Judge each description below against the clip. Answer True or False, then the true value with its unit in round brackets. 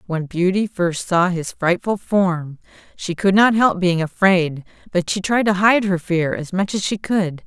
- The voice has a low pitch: False (185 Hz)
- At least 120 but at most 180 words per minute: False (200 wpm)